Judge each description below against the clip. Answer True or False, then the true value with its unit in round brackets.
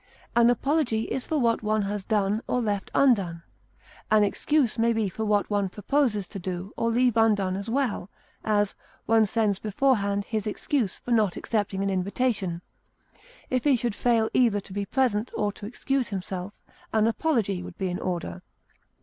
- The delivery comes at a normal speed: True (175 wpm)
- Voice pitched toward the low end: False (215 Hz)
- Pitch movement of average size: True (3.2 semitones)